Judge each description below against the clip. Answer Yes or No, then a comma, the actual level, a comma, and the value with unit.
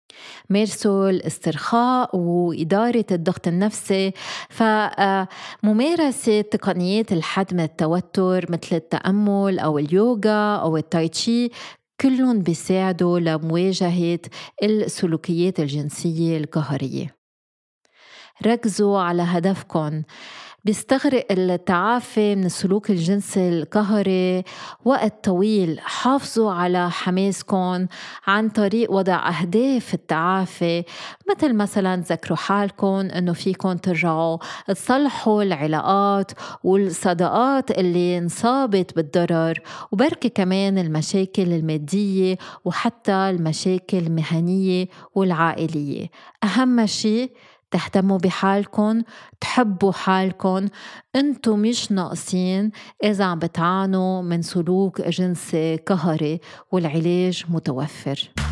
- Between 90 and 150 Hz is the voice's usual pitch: No, high, 190 Hz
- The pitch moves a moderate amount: Yes, average, 3.5 semitones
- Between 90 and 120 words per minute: No, average, 80 wpm